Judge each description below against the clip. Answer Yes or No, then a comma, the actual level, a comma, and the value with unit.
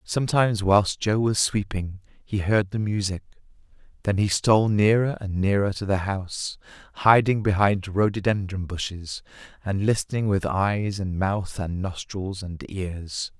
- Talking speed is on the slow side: No, average, 145 wpm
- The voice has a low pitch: Yes, low, 100 Hz